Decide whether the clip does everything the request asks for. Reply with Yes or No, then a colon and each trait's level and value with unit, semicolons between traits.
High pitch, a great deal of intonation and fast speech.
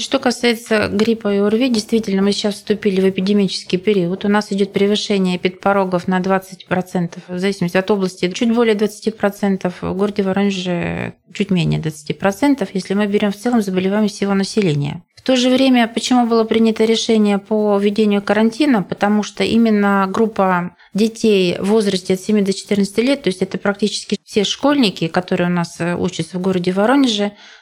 No: high, 200 Hz; average, 2.7 semitones; fast, 165 wpm